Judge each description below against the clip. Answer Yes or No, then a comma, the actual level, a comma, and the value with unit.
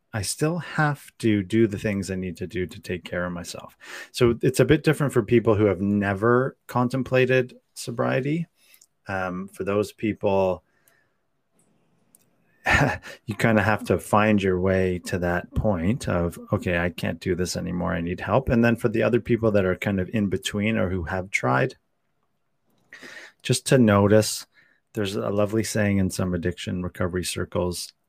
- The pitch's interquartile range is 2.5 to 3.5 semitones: No, average, 4.3 semitones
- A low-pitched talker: Yes, low, 105 Hz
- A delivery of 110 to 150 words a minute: No, average, 175 wpm